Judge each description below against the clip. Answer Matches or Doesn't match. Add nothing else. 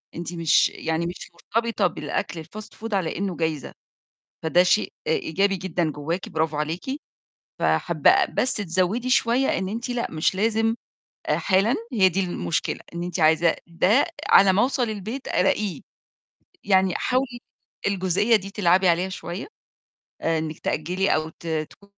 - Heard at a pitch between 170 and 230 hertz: Matches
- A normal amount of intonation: Matches